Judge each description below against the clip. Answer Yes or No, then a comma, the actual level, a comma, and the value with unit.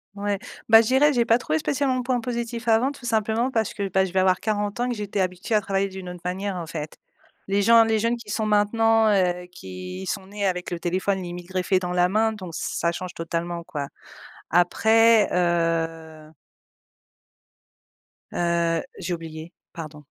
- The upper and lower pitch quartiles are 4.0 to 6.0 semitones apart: Yes, average, 4.4 semitones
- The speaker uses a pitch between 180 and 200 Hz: Yes, high, 190 Hz